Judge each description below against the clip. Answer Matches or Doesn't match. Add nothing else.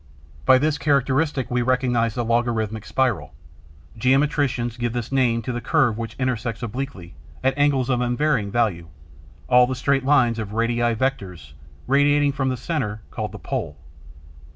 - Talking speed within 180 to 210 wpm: Doesn't match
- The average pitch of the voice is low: Matches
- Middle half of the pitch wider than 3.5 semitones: Doesn't match